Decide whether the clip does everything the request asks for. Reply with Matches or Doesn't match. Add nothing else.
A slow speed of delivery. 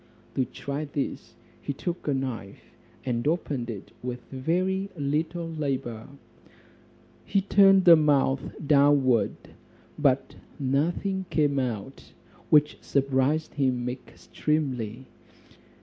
Matches